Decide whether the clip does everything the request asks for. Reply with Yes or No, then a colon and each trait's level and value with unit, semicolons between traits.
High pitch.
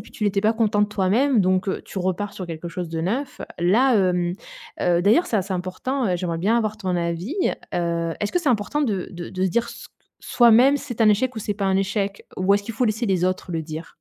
Yes: high, 200 Hz